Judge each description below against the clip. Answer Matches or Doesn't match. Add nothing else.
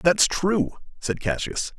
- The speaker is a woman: Doesn't match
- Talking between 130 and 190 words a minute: Matches